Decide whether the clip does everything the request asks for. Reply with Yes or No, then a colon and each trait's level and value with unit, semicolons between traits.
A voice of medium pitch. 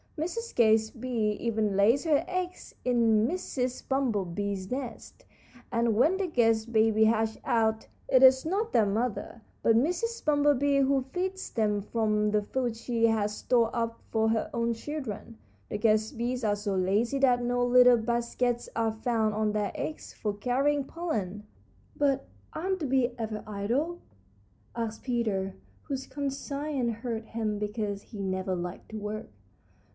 No: high, 230 Hz